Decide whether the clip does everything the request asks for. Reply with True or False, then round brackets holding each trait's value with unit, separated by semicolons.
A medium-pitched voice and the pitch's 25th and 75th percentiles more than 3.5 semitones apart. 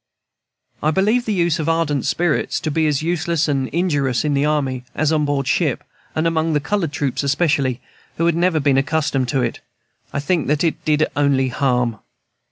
False (150 Hz; 3.1 semitones)